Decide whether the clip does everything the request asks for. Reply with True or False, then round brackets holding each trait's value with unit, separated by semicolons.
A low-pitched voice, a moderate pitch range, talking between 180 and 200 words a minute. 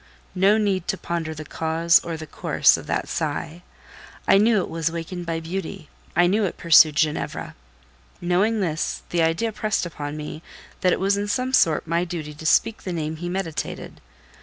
False (170 Hz; 3.3 semitones; 185 wpm)